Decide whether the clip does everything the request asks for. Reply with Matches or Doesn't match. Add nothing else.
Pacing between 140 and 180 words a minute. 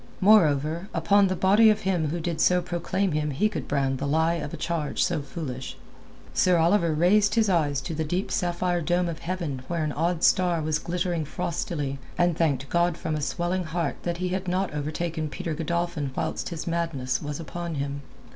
Doesn't match